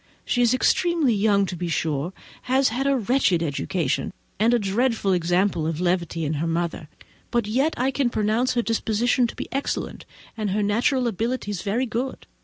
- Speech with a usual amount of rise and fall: No, wide, 5.8 semitones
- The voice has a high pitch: Yes, high, 215 Hz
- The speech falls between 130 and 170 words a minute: No, average, 180 wpm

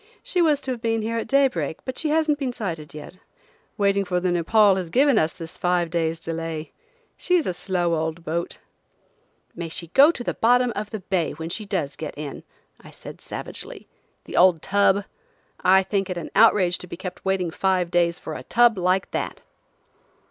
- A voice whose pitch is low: No, medium, 185 Hz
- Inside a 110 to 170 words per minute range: No, average, 195 wpm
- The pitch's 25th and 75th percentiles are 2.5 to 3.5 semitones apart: No, average, 5.2 semitones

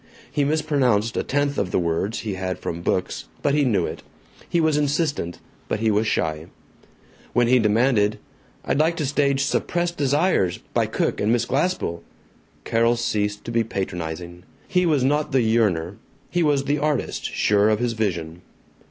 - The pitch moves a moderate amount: No, wide, 6.2 semitones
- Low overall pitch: Yes, low, 115 Hz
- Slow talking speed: No, average, 170 wpm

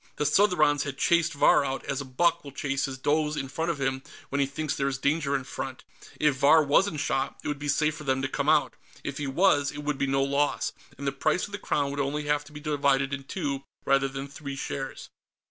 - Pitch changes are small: Yes, narrow, 1.6 semitones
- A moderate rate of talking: No, fast, 250 wpm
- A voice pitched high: No, medium, 140 Hz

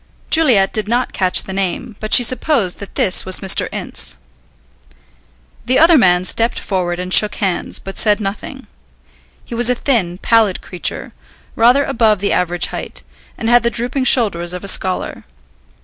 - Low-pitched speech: No, high, 210 Hz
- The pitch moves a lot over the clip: No, average, 4.6 semitones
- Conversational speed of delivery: Yes, average, 165 wpm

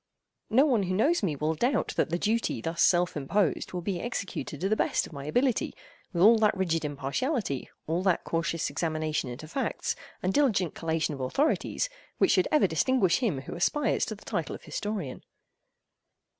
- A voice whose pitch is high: No, medium, 180 Hz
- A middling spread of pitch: No, wide, 6.1 semitones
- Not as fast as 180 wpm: No, average, 185 wpm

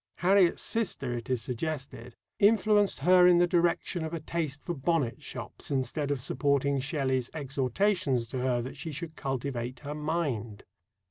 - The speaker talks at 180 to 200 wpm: No, average, 155 wpm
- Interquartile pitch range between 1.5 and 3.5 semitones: No, average, 4.8 semitones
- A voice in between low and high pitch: Yes, medium, 145 Hz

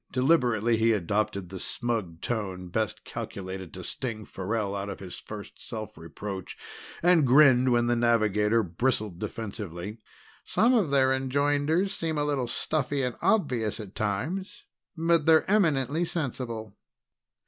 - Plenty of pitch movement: Yes, wide, 5.8 semitones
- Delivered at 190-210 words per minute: No, slow, 135 wpm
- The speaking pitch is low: Yes, low, 115 Hz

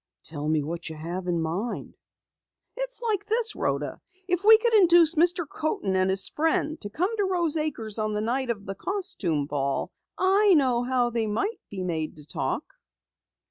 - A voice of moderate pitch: No, high, 245 Hz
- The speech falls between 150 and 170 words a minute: No, average, 180 wpm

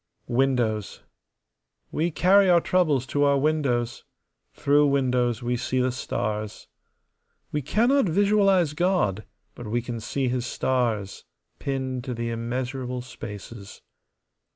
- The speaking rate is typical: No, slow, 120 wpm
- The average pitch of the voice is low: Yes, low, 130 Hz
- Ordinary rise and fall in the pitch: Yes, average, 4.2 semitones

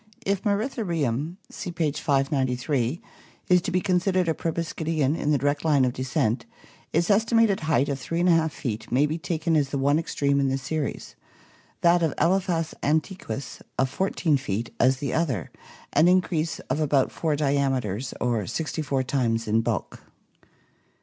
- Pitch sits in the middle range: Yes, medium, 150 Hz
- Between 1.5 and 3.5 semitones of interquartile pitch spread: No, average, 4.1 semitones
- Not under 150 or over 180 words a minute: Yes, average, 155 wpm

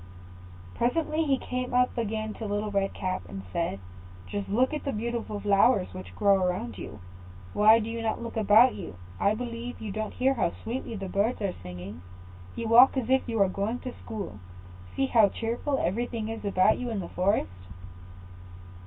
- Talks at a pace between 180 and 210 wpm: Yes, average, 190 wpm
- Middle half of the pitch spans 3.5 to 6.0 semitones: Yes, average, 3.8 semitones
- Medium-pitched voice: No, high, 215 Hz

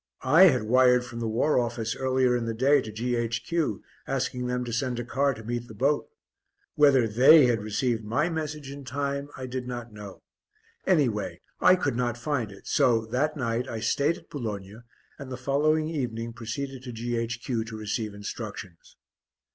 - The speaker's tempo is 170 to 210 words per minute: Yes, average, 180 wpm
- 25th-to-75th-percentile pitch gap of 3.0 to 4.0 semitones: Yes, average, 3.5 semitones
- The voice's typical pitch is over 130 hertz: No, low, 125 Hz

